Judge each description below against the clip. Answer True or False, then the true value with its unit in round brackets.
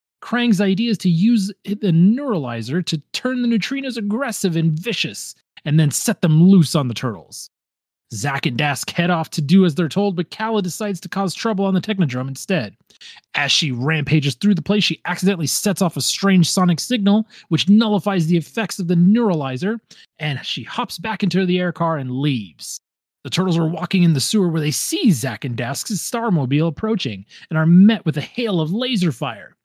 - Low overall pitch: False (180 Hz)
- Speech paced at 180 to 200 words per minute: True (195 wpm)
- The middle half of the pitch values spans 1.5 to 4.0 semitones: False (5.2 semitones)